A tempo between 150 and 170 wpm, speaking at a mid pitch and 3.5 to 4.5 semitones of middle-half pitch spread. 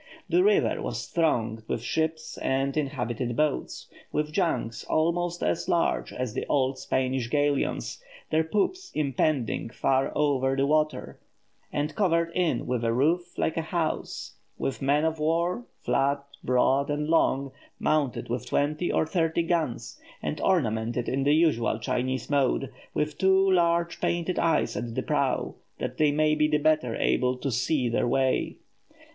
Yes: average, 155 wpm; medium, 145 Hz; average, 4.1 semitones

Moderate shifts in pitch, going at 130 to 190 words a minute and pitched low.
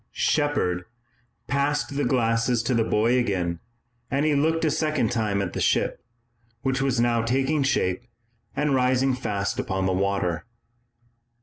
No: wide, 5.7 semitones; average, 145 wpm; low, 120 Hz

